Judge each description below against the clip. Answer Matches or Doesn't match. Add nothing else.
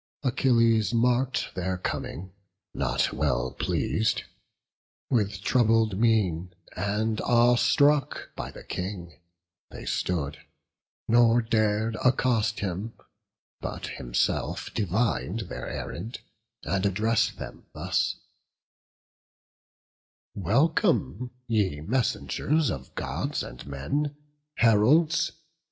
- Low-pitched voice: Matches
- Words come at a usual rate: Doesn't match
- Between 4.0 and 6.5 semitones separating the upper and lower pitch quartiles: Matches